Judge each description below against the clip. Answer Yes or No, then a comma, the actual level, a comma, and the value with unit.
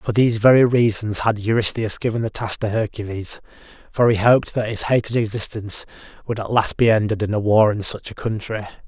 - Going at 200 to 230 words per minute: Yes, fast, 205 wpm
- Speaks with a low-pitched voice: Yes, low, 110 Hz